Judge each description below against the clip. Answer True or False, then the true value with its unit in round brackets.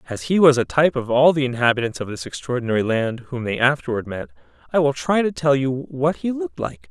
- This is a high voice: False (130 Hz)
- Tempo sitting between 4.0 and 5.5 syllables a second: False (6.2 syllables/s)